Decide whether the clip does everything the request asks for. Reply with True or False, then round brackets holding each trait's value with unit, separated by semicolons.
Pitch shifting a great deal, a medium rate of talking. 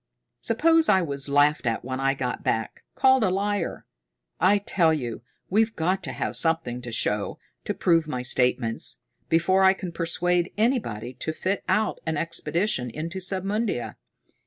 True (6.9 semitones; 160 wpm)